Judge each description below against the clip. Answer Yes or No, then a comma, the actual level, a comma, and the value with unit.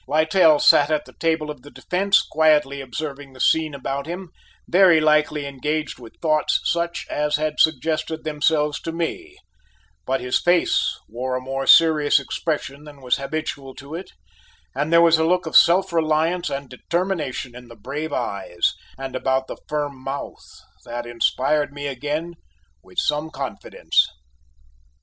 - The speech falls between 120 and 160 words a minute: Yes, average, 155 wpm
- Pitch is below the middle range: No, medium, 150 Hz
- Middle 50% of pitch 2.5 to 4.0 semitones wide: Yes, average, 2.9 semitones